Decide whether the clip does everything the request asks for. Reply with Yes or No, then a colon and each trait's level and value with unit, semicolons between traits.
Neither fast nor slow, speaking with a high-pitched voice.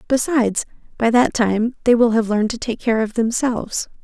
Yes: average, 195 wpm; high, 230 Hz